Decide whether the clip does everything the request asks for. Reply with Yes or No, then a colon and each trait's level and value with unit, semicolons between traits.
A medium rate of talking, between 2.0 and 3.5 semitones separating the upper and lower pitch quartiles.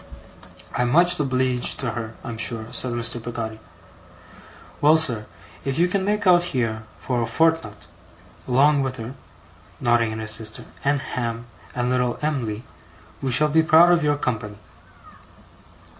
No: average, 150 wpm; average, 4.7 semitones